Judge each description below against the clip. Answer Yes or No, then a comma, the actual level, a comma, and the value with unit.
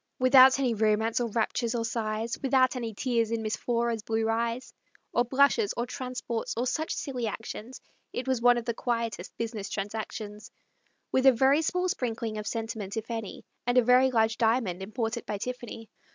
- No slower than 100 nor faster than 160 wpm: No, average, 180 wpm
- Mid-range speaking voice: No, high, 235 Hz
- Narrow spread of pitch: Yes, narrow, 2.3 semitones